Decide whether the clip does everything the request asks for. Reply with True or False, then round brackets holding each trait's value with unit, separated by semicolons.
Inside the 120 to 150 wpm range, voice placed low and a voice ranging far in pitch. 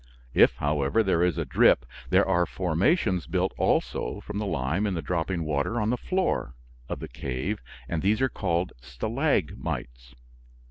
False (165 wpm; 90 Hz; 6.8 semitones)